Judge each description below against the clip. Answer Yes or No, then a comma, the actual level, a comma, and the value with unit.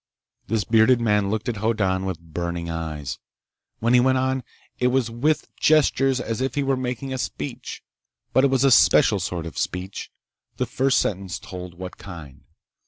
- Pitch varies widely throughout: Yes, wide, 6.2 semitones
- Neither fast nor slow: Yes, average, 175 wpm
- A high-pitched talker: No, low, 110 Hz